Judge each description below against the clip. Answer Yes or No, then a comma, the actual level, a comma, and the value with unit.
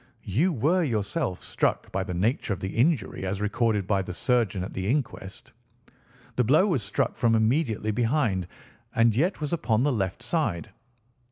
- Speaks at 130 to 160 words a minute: No, average, 170 wpm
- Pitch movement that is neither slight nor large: No, wide, 5.9 semitones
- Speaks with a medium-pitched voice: No, low, 110 Hz